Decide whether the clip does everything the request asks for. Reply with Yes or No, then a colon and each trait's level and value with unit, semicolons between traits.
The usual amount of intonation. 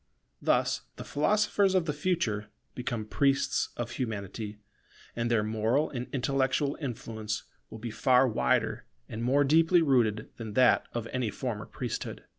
Yes: average, 4.4 semitones